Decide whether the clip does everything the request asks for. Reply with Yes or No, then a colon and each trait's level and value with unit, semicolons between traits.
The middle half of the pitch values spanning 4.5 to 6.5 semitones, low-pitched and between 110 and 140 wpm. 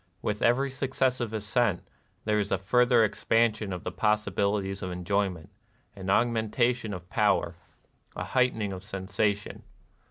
No: average, 3.4 semitones; low, 105 Hz; slow, 135 wpm